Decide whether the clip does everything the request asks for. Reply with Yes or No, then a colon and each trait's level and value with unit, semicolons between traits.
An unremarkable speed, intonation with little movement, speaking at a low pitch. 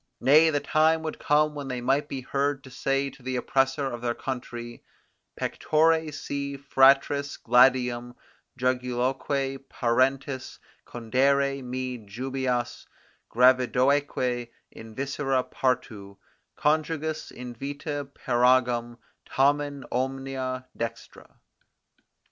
No: slow, 100 wpm; narrow, 2.1 semitones; low, 130 Hz